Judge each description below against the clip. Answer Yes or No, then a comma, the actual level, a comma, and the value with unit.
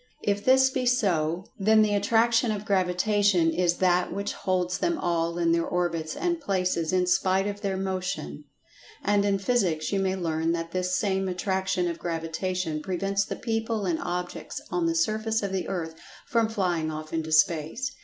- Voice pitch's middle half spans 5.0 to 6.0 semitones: No, average, 3.3 semitones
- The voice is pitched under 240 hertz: Yes, medium, 185 Hz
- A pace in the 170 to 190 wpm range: Yes, average, 180 wpm